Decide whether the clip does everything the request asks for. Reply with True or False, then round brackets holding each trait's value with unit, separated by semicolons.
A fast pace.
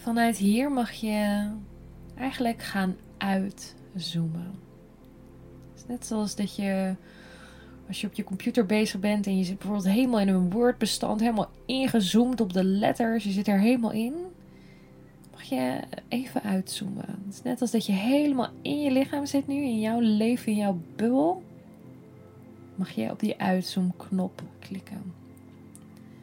False (145 wpm)